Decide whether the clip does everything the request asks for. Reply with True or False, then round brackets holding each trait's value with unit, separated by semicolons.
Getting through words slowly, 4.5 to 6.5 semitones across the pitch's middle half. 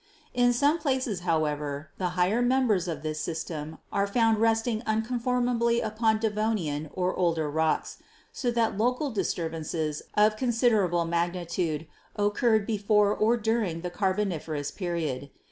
True (130 wpm; 5.5 semitones)